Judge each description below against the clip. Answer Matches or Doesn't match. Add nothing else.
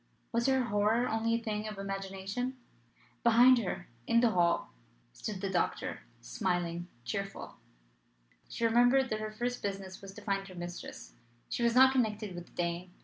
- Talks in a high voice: Matches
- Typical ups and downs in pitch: Matches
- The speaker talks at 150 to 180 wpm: Matches